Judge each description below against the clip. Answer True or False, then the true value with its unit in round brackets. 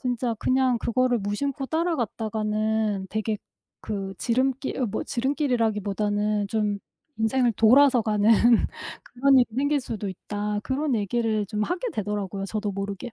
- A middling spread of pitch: True (3.6 semitones)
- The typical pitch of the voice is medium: False (220 Hz)